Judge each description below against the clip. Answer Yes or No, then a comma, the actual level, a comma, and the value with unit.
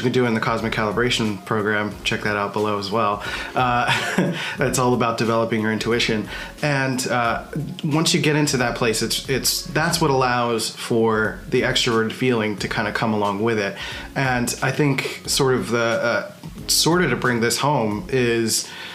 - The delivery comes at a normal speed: Yes, average, 190 wpm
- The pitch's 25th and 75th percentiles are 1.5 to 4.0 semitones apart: Yes, average, 3.4 semitones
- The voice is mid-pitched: No, low, 120 Hz